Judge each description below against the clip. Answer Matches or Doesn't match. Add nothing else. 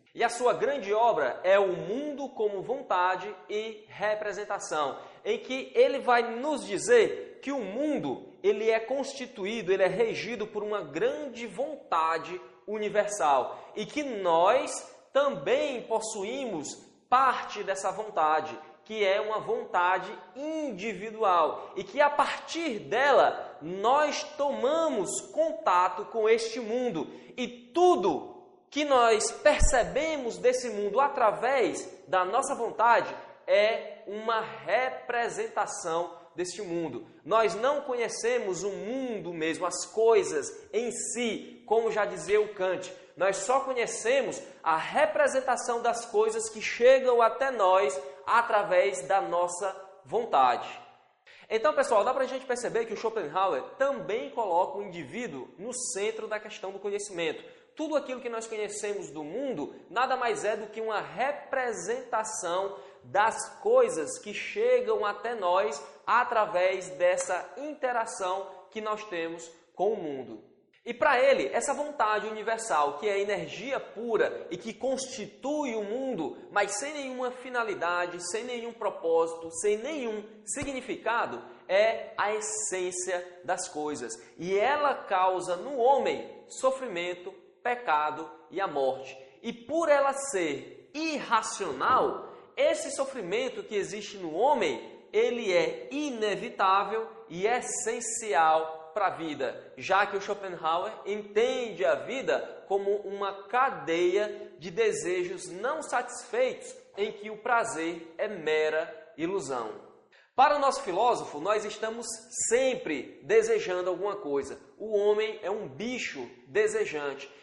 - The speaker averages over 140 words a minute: Doesn't match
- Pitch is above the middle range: Matches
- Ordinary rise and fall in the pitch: Doesn't match